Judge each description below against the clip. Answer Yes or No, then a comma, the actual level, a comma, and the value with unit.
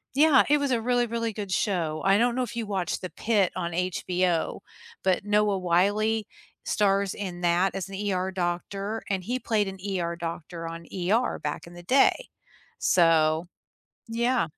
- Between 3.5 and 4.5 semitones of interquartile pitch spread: Yes, average, 4.1 semitones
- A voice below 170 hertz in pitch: No, high, 195 Hz